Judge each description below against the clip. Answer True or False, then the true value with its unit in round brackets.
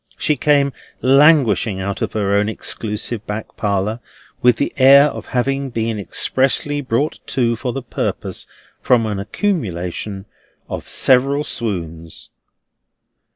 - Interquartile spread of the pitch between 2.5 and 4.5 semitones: False (5.0 semitones)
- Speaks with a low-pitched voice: True (115 Hz)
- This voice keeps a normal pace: False (125 wpm)